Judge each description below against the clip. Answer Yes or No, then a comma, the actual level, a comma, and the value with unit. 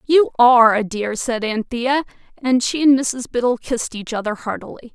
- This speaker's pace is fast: No, average, 180 wpm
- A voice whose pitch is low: No, high, 245 Hz